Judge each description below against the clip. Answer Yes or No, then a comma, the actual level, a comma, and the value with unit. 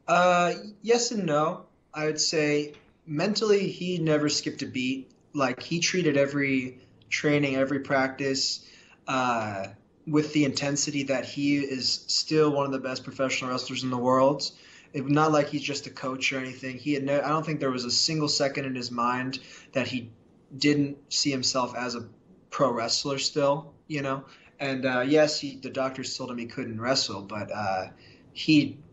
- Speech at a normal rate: Yes, average, 180 wpm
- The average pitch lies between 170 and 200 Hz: No, medium, 140 Hz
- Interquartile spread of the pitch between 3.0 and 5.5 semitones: No, narrow, 2.5 semitones